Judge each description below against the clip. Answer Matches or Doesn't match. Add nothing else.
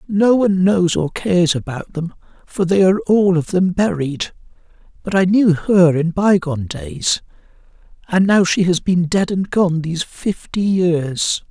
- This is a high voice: Doesn't match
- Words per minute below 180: Matches